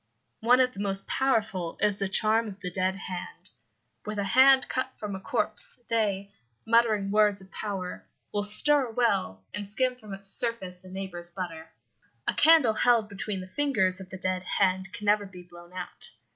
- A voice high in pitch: Yes, high, 200 Hz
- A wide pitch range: No, average, 3.3 semitones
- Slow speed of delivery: No, average, 185 wpm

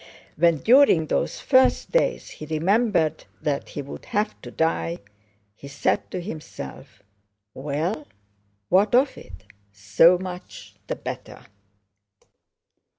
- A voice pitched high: No, medium, 160 Hz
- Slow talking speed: Yes, slow, 115 wpm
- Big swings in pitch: Yes, wide, 6.4 semitones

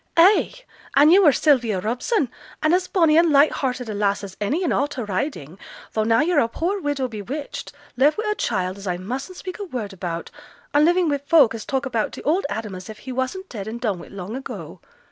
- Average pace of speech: No, fast, 230 wpm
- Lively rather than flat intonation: Yes, wide, 6.7 semitones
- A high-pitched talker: Yes, very high, 260 Hz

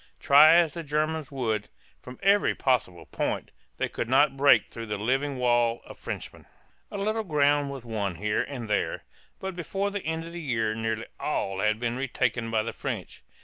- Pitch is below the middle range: Yes, low, 130 Hz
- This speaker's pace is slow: No, average, 190 wpm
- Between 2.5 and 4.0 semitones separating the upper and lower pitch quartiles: No, wide, 5.5 semitones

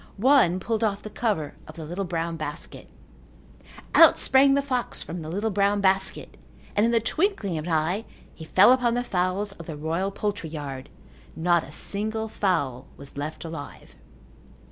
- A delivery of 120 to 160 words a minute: No, average, 175 wpm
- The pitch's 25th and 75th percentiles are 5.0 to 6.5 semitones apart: Yes, average, 5.3 semitones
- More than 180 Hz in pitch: Yes, high, 190 Hz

